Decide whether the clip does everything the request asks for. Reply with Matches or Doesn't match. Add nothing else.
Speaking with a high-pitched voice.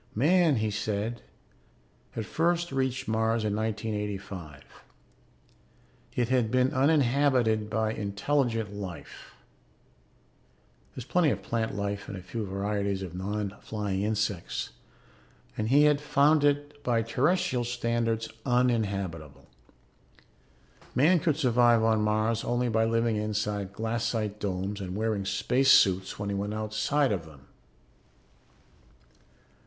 Doesn't match